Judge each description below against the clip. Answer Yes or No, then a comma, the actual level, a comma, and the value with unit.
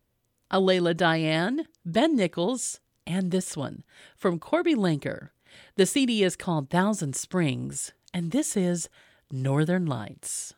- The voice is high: No, medium, 180 Hz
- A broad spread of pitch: No, average, 3.7 semitones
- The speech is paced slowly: Yes, slow, 120 wpm